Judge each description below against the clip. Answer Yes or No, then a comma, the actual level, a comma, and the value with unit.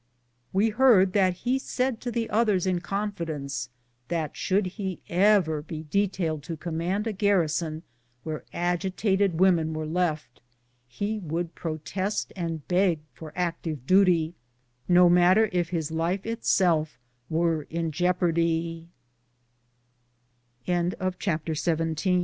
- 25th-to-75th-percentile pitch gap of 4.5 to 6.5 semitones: No, average, 3.3 semitones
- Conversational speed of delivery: No, slow, 115 wpm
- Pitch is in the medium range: Yes, medium, 175 Hz